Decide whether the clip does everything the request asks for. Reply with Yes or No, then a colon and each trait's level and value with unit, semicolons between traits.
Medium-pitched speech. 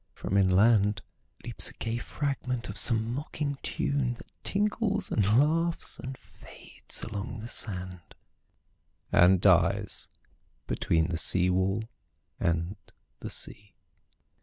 No: low, 110 Hz